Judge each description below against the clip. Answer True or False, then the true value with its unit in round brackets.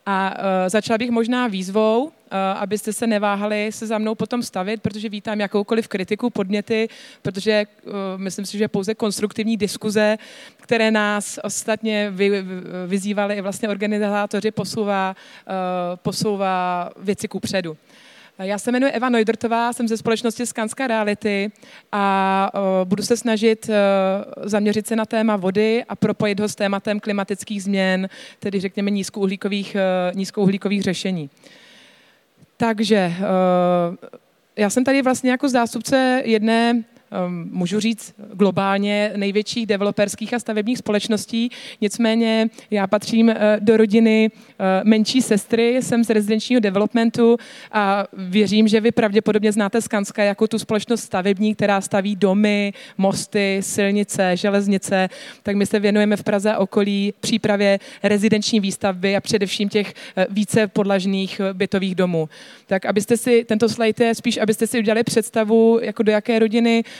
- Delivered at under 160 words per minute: True (130 wpm)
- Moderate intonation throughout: False (2.1 semitones)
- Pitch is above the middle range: True (210 Hz)